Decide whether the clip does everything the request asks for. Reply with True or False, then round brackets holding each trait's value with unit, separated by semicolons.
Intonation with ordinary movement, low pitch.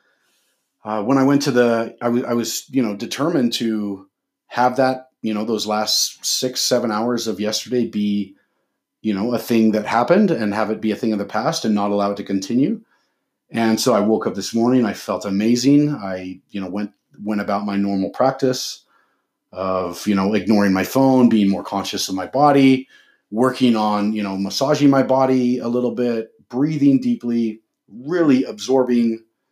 True (3.6 semitones; 115 Hz)